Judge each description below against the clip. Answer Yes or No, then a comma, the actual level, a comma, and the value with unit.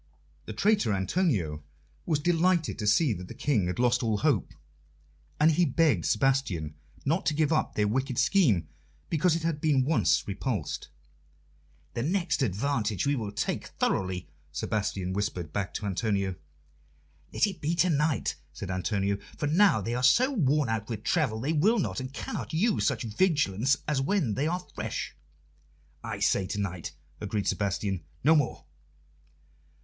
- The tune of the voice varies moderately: No, wide, 7.7 semitones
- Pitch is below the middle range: Yes, low, 125 Hz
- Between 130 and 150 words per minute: No, average, 160 wpm